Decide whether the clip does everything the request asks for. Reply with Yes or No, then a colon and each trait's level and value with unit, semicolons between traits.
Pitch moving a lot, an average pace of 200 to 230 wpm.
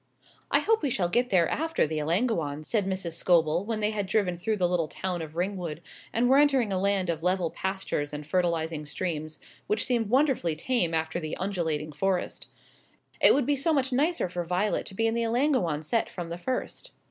Yes: wide, 5.8 semitones; fast, 205 wpm